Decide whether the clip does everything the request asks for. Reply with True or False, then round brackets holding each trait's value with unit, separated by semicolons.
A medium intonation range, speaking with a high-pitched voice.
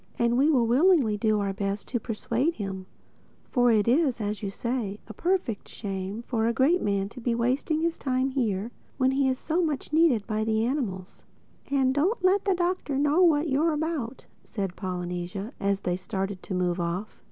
False (6.4 semitones; 235 Hz)